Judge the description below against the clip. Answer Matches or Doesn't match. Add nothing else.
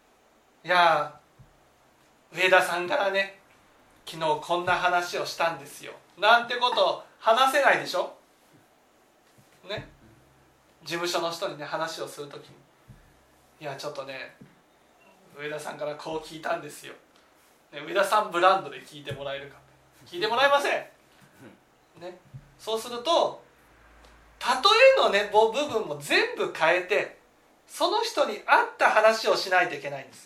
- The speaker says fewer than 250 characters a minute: Doesn't match